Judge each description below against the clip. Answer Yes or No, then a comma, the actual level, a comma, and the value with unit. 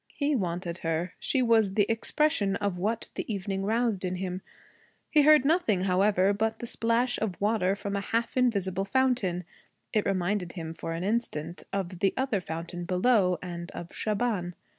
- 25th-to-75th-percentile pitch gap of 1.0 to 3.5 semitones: No, average, 4.1 semitones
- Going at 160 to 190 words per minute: Yes, average, 170 wpm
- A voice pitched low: No, high, 200 Hz